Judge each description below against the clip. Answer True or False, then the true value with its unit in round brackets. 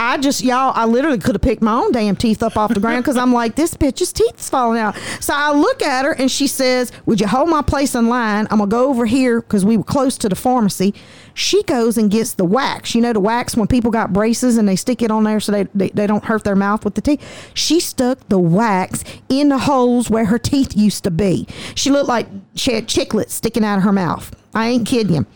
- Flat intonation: False (3.8 semitones)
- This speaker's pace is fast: True (265 wpm)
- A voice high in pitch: True (235 Hz)